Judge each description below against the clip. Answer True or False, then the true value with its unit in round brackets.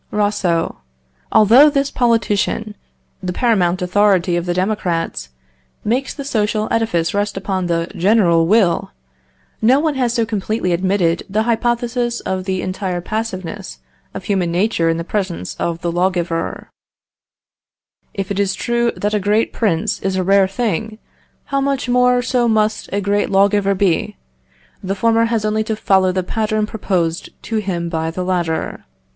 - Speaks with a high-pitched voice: True (200 Hz)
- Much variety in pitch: False (3.7 semitones)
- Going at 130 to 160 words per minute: True (155 wpm)